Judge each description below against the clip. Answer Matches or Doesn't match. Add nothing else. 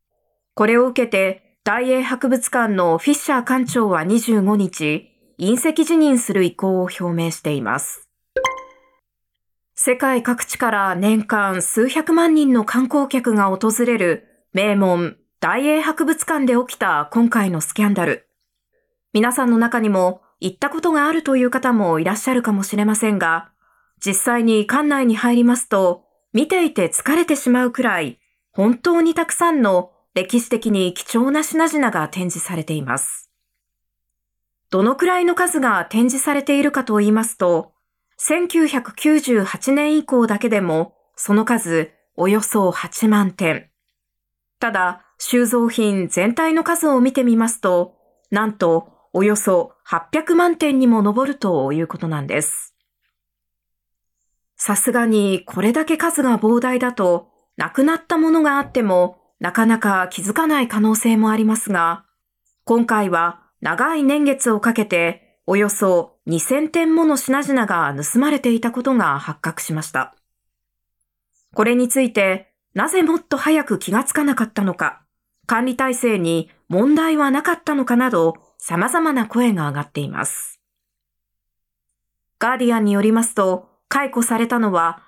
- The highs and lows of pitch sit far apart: Matches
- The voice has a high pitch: Matches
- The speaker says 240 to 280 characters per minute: Matches